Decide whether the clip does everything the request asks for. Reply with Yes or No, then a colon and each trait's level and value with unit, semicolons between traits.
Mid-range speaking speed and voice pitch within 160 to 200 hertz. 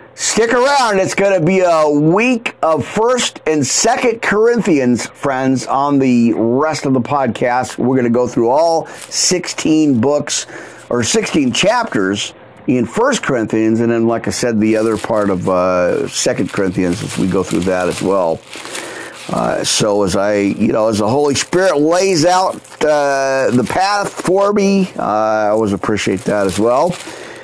No: average, 170 wpm; medium, 140 Hz